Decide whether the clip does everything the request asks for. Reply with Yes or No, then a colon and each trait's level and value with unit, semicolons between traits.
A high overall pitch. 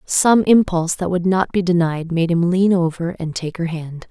No: medium, 175 Hz